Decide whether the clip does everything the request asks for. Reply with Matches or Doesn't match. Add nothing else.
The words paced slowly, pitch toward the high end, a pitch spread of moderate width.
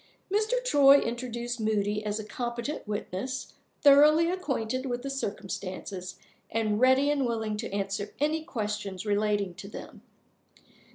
Matches